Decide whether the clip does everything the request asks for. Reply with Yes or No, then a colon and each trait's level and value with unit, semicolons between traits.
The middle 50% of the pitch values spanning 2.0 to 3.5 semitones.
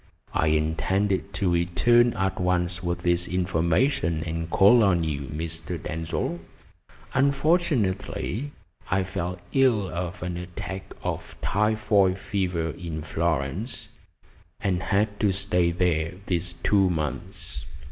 Yes: average, 3.1 semitones